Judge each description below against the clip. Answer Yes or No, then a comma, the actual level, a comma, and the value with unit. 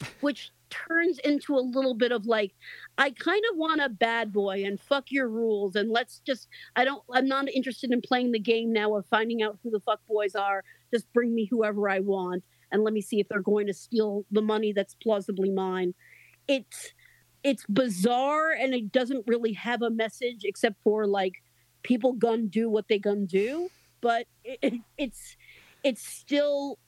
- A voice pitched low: No, high, 230 Hz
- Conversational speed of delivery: Yes, average, 190 wpm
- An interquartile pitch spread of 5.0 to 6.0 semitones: No, average, 4.0 semitones